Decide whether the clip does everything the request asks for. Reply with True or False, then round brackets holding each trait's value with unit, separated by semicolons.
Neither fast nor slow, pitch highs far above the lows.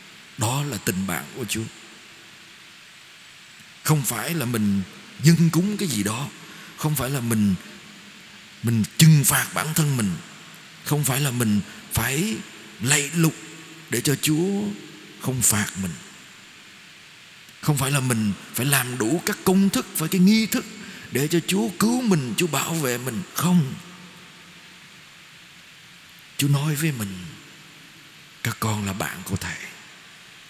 False (140 wpm; 6.6 semitones)